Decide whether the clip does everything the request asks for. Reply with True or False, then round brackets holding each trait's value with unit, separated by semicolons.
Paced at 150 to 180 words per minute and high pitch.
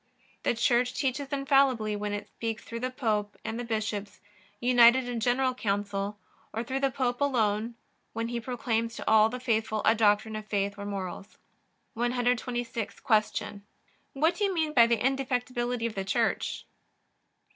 True (160 wpm; 235 Hz)